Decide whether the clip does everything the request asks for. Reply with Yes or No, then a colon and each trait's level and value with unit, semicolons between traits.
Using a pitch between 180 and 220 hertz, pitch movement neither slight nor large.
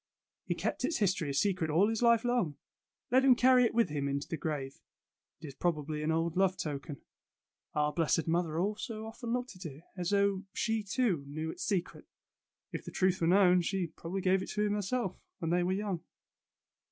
Yes: medium, 185 Hz; average, 4.6 semitones